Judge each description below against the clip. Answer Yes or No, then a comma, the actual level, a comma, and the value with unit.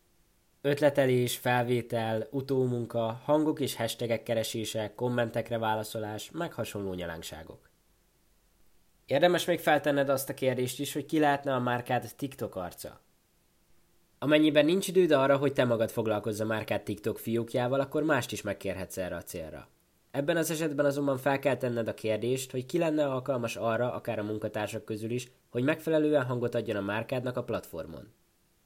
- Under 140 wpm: No, average, 150 wpm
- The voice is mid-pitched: No, low, 125 Hz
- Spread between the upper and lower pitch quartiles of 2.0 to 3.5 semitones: No, average, 4.2 semitones